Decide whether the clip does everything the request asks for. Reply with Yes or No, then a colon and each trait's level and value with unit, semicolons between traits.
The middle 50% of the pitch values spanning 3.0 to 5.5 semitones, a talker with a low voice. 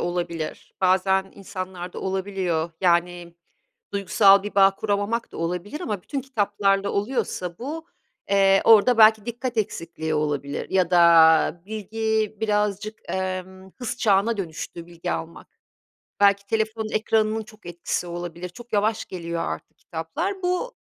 No: average, 3.8 semitones; high, 195 Hz